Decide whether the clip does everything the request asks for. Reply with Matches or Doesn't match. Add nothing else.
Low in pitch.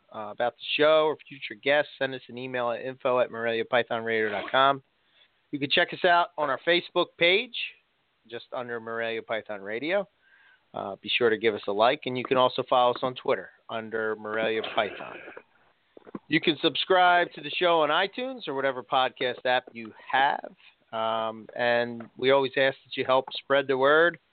Matches